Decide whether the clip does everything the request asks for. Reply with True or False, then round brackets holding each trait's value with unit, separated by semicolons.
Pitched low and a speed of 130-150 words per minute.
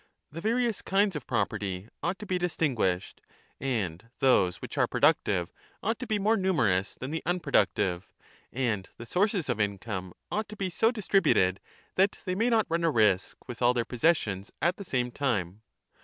False (130 Hz; 180 wpm)